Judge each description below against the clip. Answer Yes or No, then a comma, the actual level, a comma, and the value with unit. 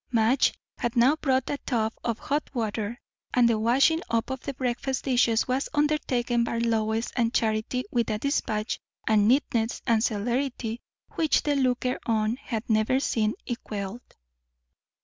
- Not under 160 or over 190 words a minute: No, average, 150 wpm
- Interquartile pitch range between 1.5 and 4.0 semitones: Yes, average, 2.9 semitones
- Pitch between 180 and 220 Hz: No, high, 235 Hz